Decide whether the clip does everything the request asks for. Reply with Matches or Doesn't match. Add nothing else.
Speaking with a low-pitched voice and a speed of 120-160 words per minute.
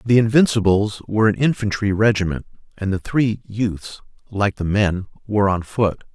Matches